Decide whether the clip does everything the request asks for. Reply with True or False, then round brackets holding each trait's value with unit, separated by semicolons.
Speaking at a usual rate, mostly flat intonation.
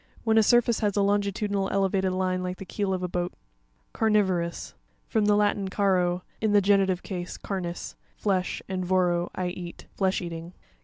True (165 wpm; 2.1 semitones)